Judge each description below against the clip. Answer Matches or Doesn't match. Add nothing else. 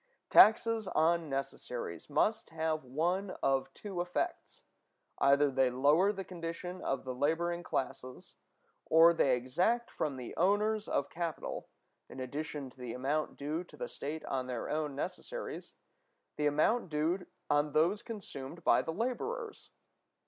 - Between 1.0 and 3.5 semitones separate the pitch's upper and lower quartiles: Doesn't match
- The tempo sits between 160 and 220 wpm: Doesn't match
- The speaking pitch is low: Doesn't match